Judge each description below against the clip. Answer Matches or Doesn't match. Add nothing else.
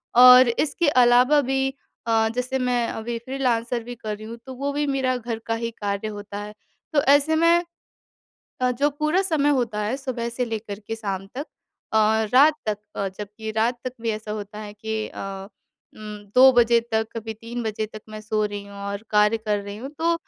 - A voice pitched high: Matches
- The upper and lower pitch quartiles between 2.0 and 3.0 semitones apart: Doesn't match